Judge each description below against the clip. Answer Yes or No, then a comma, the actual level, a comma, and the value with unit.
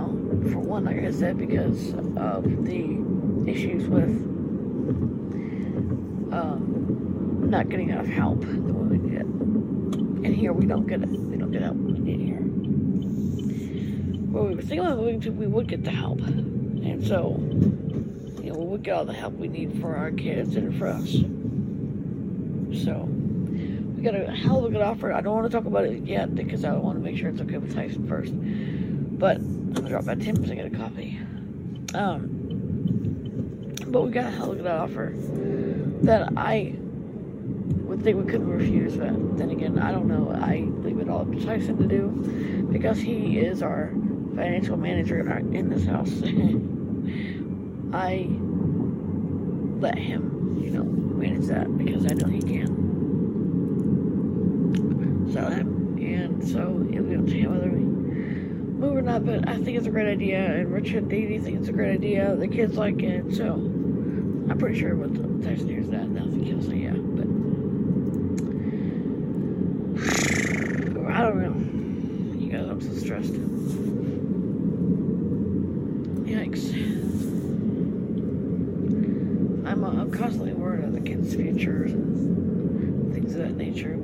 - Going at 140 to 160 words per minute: Yes, average, 155 wpm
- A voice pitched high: Yes, high, 210 Hz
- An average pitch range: No, narrow, 1.7 semitones